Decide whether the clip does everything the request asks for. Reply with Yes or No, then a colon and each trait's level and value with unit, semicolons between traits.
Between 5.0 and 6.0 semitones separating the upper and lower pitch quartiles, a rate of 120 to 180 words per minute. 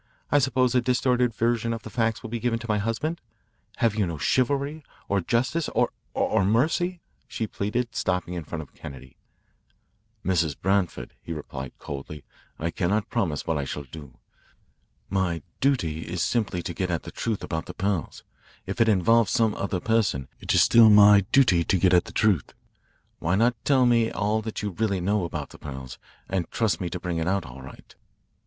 No: wide, 5.4 semitones; average, 190 wpm